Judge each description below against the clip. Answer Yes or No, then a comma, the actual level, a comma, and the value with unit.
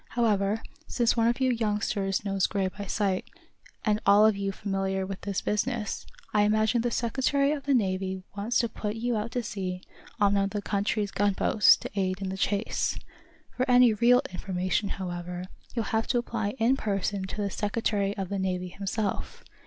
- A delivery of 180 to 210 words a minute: Yes, average, 190 wpm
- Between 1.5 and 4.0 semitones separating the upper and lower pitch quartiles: Yes, average, 2.7 semitones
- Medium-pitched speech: No, high, 205 Hz